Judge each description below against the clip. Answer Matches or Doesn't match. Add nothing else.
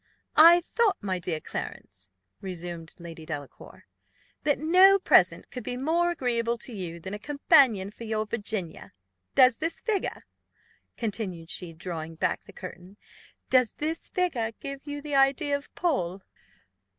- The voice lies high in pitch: Matches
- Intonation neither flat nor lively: Doesn't match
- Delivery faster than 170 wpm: Doesn't match